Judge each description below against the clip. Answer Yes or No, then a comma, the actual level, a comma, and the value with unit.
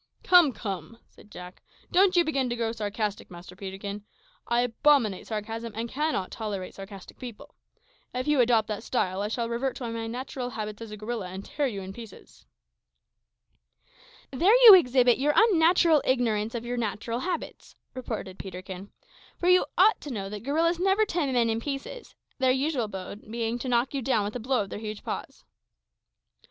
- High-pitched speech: Yes, high, 235 Hz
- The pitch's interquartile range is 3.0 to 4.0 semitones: No, average, 4.7 semitones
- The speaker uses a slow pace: No, average, 180 wpm